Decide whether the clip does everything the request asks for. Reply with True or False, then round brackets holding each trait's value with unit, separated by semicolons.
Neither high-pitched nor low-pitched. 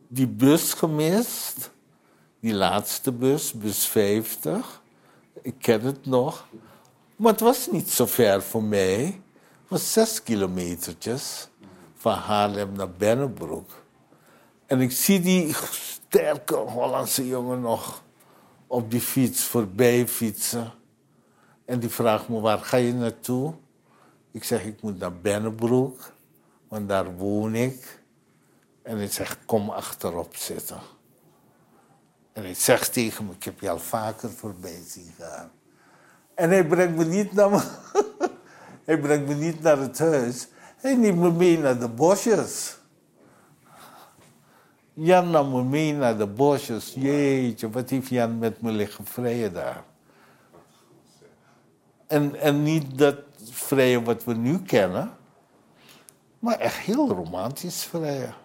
False (125 Hz)